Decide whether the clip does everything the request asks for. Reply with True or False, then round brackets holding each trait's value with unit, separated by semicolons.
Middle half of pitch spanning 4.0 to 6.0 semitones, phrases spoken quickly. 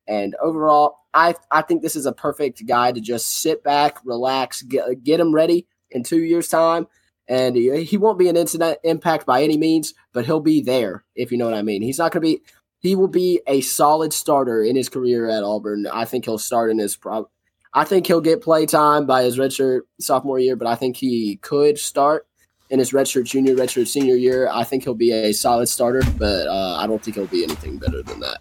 True (4.6 semitones; 225 wpm)